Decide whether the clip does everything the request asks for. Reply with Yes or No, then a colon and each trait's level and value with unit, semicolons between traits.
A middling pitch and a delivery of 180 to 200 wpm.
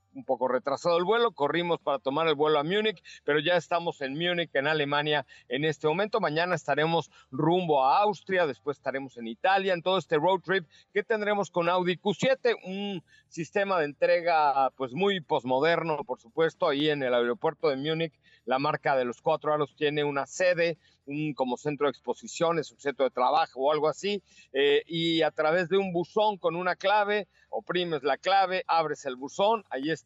Yes: medium, 160 Hz; fast, 190 wpm